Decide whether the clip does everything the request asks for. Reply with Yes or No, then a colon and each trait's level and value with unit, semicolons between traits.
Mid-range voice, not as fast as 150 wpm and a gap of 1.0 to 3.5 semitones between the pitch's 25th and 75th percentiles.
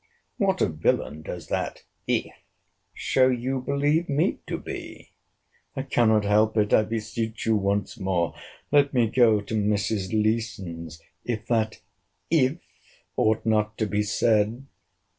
No: low, 110 Hz; slow, 135 wpm; average, 3.0 semitones